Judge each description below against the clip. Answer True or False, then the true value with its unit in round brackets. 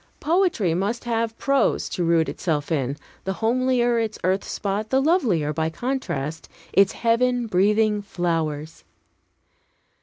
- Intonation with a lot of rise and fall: True (6.5 semitones)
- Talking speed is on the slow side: True (125 wpm)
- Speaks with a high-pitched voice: True (210 Hz)